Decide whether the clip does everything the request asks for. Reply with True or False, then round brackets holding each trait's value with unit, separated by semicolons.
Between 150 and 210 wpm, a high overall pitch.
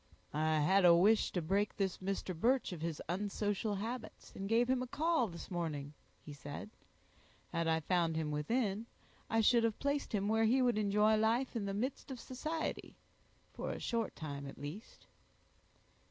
True (180 wpm; 205 Hz)